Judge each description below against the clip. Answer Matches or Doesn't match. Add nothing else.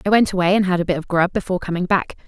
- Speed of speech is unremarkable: Doesn't match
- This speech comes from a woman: Matches